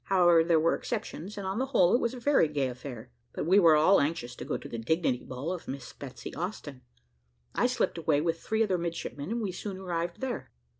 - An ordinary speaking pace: No, fast, 230 wpm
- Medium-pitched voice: Yes, medium, 170 Hz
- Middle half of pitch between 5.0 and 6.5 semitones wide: Yes, average, 5.3 semitones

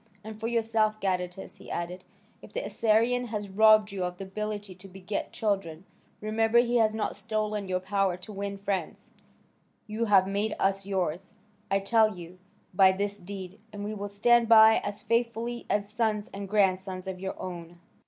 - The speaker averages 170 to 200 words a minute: Yes, average, 175 wpm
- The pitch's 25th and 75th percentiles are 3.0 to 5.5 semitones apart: No, narrow, 2.4 semitones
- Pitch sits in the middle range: No, high, 205 Hz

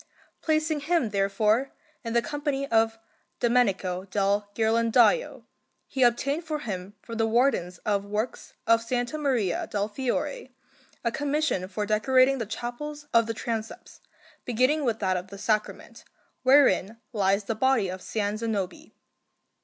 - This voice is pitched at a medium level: No, high, 230 Hz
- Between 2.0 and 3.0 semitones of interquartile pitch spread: No, average, 4.5 semitones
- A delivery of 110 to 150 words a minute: Yes, average, 140 wpm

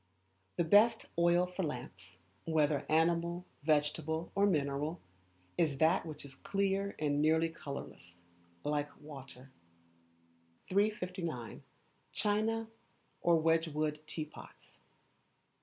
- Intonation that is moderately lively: Yes, average, 3.3 semitones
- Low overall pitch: No, medium, 160 Hz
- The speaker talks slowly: Yes, slow, 95 wpm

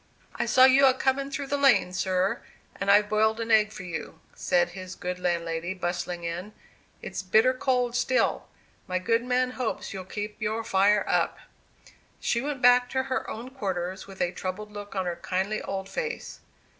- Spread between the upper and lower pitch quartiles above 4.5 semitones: Yes, average, 5.3 semitones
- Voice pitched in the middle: No, high, 210 Hz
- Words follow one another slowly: No, average, 180 wpm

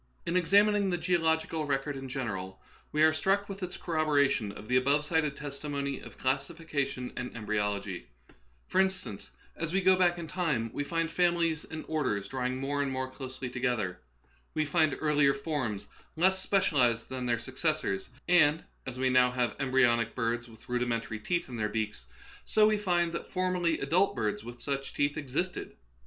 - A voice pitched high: No, medium, 140 Hz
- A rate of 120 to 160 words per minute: No, average, 175 wpm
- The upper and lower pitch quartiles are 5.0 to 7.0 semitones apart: Yes, average, 5.3 semitones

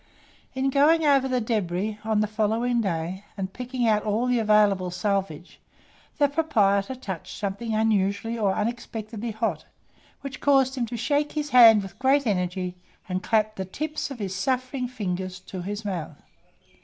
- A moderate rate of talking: Yes, average, 160 wpm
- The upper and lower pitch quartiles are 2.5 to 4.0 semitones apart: No, average, 4.6 semitones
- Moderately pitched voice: No, high, 215 Hz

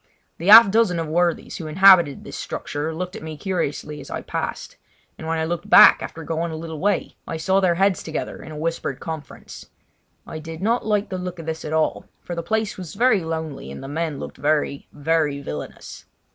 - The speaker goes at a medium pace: No, fast, 215 wpm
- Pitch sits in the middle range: Yes, medium, 165 Hz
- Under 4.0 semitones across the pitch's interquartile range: Yes, average, 2.9 semitones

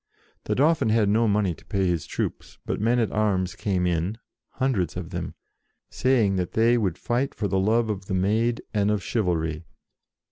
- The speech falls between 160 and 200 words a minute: Yes, average, 185 wpm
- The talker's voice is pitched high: No, low, 105 Hz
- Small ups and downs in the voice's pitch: No, average, 3.8 semitones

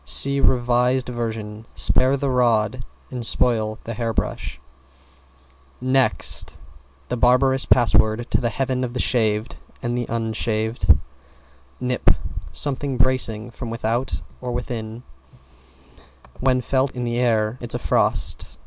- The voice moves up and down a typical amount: No, narrow, 2.2 semitones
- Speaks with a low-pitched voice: Yes, low, 120 Hz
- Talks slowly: Yes, slow, 125 wpm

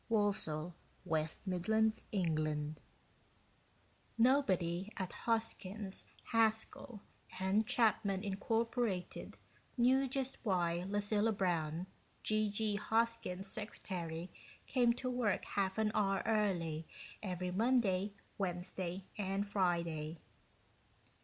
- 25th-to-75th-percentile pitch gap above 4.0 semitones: No, average, 3.7 semitones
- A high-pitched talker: Yes, high, 200 Hz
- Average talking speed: No, slow, 85 wpm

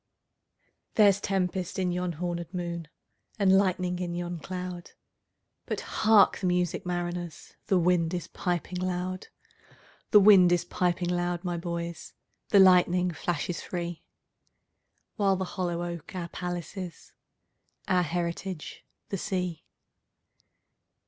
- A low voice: No, medium, 180 Hz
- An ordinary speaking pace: No, slow, 100 wpm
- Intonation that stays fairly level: Yes, narrow, 1.2 semitones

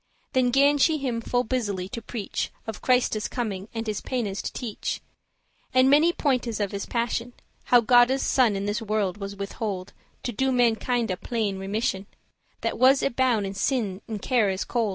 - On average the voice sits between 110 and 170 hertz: No, high, 230 Hz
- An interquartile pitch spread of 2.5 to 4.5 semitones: Yes, average, 3.8 semitones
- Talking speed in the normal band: Yes, average, 180 wpm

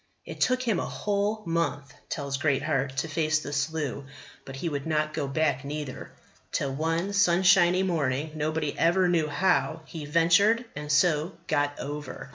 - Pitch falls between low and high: Yes, medium, 155 Hz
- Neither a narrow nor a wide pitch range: Yes, average, 3.4 semitones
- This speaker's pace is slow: No, average, 160 wpm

